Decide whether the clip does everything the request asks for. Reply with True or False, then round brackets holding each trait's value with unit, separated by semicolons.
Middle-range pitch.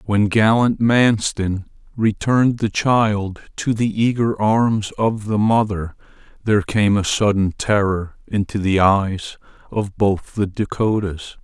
False (105 Hz)